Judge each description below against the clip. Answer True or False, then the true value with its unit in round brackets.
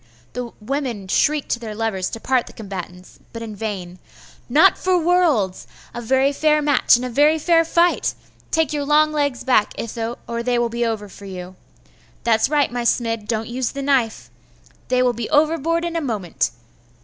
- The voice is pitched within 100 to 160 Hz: False (245 Hz)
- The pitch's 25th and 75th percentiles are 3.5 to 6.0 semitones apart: True (5.1 semitones)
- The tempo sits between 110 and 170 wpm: False (185 wpm)